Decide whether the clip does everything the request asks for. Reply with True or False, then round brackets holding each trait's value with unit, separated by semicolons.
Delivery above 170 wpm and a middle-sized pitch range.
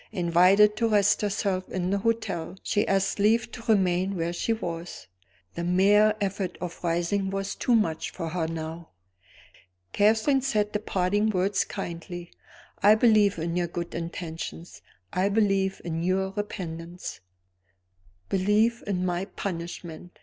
False (140 wpm; 3.2 semitones)